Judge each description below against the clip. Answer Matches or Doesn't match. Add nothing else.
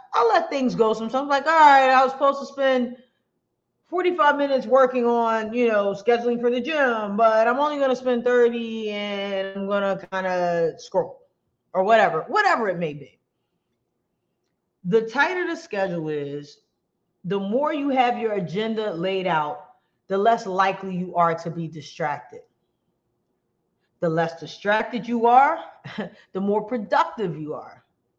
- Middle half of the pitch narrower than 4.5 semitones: Doesn't match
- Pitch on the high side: Matches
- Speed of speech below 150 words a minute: Doesn't match